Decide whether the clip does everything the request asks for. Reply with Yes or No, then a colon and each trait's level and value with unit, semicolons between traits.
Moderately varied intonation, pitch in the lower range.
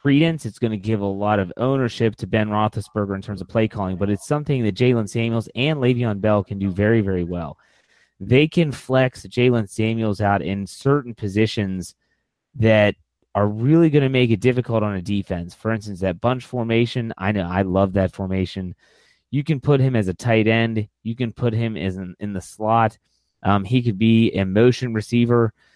Yes: average, 3.3 semitones; low, 110 Hz